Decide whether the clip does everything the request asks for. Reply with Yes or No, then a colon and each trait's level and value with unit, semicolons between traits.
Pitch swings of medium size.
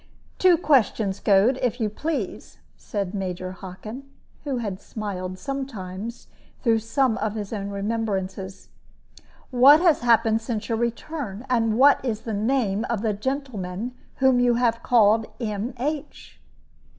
Yes: average, 4.0 semitones